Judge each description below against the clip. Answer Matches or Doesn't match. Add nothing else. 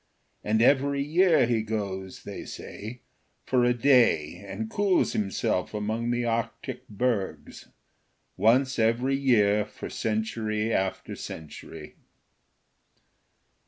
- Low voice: Matches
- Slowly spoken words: Matches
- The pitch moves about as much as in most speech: Matches